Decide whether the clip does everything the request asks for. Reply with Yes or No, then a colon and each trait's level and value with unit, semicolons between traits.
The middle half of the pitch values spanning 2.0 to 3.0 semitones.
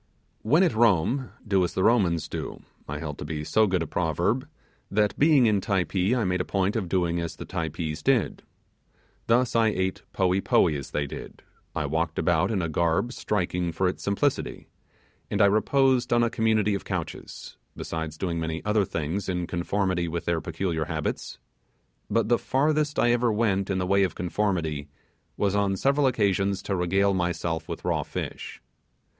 No: average, 4.4 semitones